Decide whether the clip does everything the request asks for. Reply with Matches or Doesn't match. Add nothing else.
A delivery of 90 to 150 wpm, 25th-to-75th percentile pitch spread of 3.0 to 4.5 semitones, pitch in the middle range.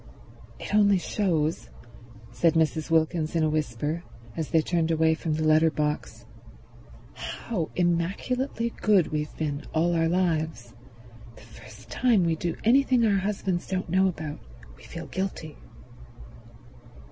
Matches